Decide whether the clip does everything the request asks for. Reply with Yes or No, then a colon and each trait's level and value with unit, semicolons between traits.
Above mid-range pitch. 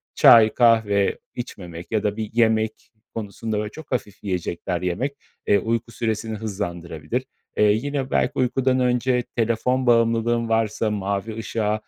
No: low, 110 Hz